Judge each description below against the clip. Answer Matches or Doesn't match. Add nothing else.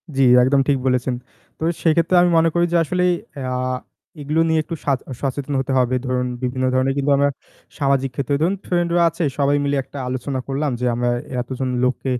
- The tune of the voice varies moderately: Matches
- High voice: Doesn't match